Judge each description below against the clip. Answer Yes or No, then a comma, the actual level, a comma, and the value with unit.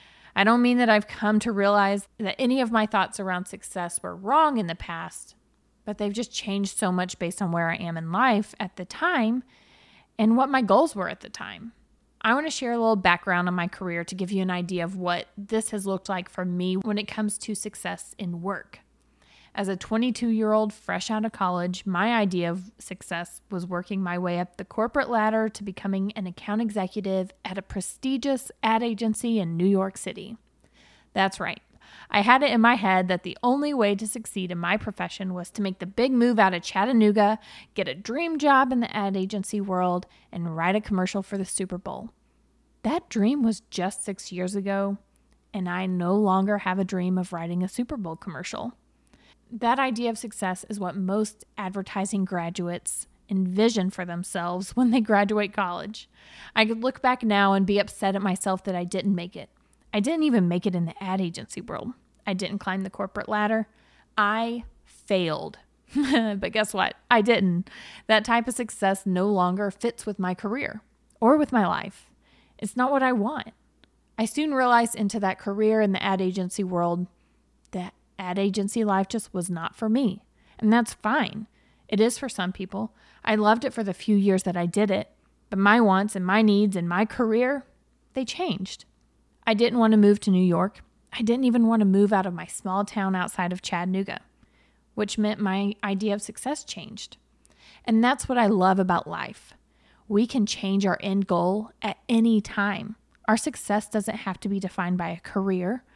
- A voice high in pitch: Yes, high, 205 Hz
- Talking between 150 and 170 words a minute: No, average, 200 wpm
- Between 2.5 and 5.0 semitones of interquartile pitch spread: Yes, average, 3.1 semitones